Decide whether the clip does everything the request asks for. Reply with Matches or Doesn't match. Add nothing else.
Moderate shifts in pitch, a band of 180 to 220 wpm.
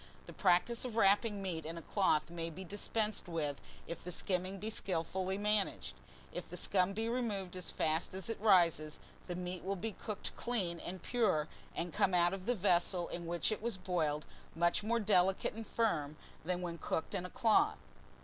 Matches